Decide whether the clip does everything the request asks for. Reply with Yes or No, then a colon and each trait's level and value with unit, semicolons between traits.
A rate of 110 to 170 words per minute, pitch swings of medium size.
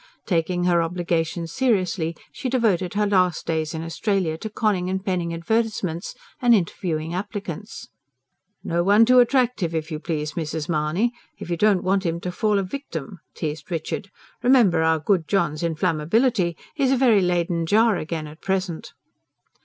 Yes: average, 160 wpm; average, 4.2 semitones